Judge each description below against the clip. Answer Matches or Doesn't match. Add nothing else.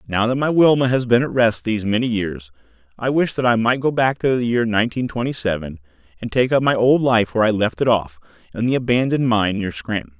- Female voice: Doesn't match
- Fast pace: Matches